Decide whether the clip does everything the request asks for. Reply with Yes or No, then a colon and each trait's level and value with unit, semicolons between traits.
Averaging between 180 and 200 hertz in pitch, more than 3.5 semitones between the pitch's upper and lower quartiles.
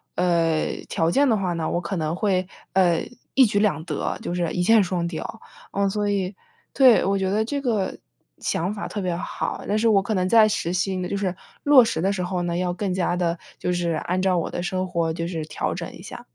No: medium, 185 Hz; average, 2.8 semitones